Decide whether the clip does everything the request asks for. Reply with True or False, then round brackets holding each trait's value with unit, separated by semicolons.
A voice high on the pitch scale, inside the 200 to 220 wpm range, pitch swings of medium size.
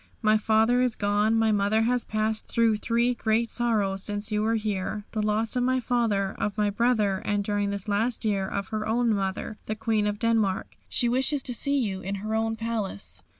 False (215 Hz; 205 wpm; 2.1 semitones)